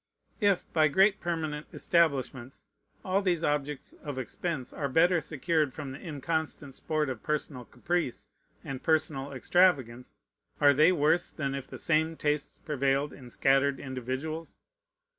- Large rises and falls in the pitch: No, average, 3.2 semitones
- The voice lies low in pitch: No, medium, 150 Hz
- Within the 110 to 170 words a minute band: Yes, average, 140 wpm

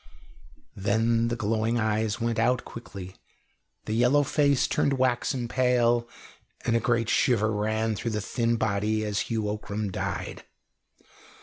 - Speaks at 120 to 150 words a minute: Yes, slow, 135 wpm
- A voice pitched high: No, low, 115 Hz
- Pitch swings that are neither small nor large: No, narrow, 2.0 semitones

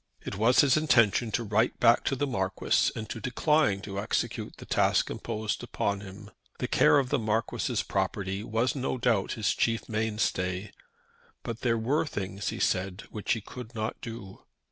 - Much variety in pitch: No, average, 3.4 semitones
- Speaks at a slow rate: No, average, 175 wpm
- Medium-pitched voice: No, low, 110 Hz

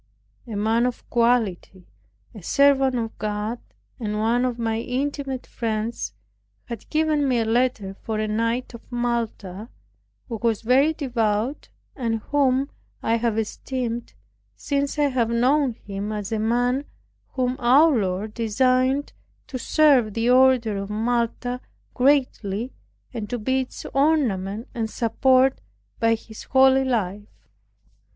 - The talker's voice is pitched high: Yes, high, 235 Hz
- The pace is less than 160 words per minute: Yes, slow, 135 wpm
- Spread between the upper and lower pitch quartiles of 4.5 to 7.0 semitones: No, average, 3.0 semitones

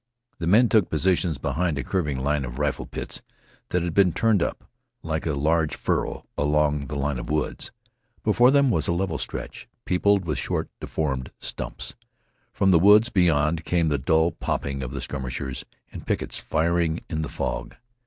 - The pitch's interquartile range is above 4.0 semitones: No, average, 3.7 semitones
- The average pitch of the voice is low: Yes, very low, 80 Hz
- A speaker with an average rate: Yes, average, 175 wpm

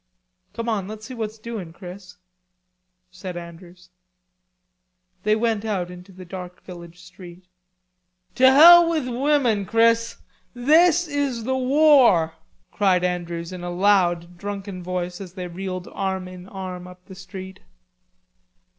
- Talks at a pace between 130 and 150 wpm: Yes, slow, 135 wpm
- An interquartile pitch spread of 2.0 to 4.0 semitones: No, average, 4.4 semitones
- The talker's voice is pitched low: No, high, 190 Hz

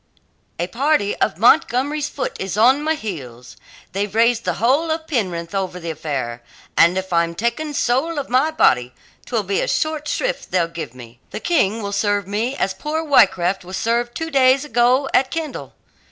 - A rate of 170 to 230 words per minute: Yes, average, 180 wpm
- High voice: Yes, high, 225 Hz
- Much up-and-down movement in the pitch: Yes, wide, 7.7 semitones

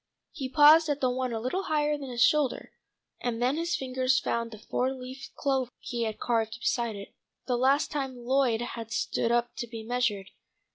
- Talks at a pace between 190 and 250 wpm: Yes, average, 195 wpm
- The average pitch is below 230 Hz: No, very high, 250 Hz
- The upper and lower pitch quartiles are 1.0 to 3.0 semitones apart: Yes, narrow, 2.6 semitones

